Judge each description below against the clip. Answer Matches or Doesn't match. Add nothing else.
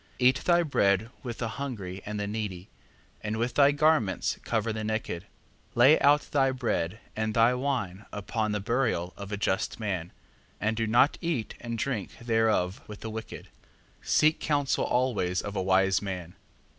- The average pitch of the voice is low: Matches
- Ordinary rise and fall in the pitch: Matches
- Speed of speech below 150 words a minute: Doesn't match